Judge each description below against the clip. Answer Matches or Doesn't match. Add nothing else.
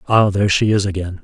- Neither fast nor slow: Doesn't match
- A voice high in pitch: Doesn't match